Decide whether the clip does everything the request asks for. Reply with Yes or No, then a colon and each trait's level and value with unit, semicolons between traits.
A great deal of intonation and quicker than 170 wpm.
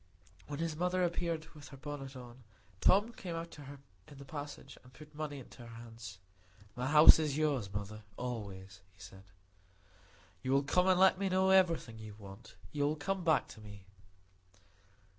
Yes: wide, 6.3 semitones; average, 180 wpm